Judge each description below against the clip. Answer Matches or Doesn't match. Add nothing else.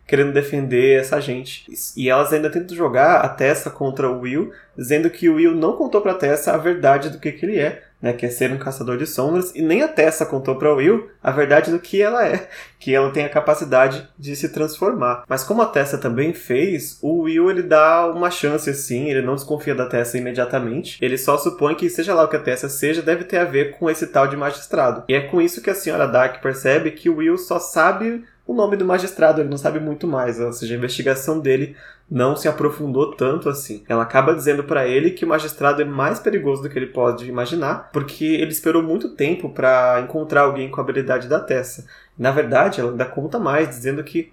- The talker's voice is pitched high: Doesn't match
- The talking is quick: Matches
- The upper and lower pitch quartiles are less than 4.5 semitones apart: Matches